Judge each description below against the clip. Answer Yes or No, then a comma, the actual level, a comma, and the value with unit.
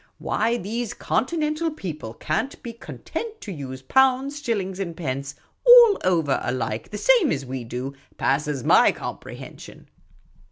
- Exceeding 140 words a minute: No, slow, 135 wpm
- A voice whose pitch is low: No, high, 190 Hz